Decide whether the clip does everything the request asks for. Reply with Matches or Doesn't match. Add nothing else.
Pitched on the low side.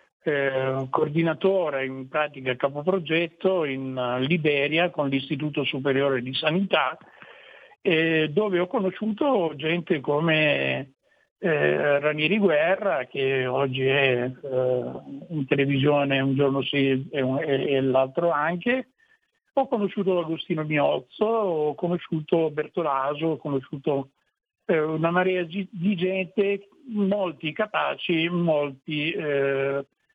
Doesn't match